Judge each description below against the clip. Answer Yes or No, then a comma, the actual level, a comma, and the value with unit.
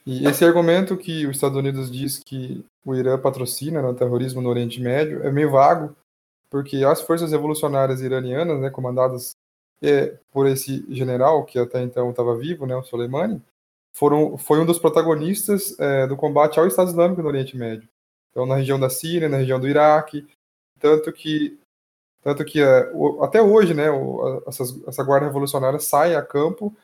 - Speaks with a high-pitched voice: No, medium, 140 Hz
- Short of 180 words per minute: Yes, average, 170 wpm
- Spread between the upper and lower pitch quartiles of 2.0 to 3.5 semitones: Yes, average, 3.1 semitones